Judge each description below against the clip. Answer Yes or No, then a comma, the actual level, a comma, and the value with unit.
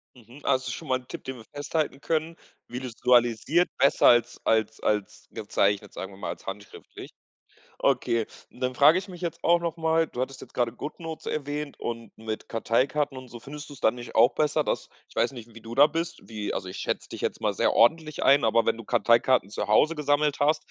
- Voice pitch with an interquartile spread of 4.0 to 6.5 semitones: Yes, average, 4.6 semitones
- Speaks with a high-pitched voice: No, low, 130 Hz